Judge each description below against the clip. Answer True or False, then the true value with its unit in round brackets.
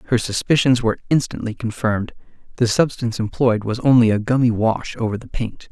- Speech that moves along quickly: False (170 wpm)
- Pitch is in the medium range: False (115 Hz)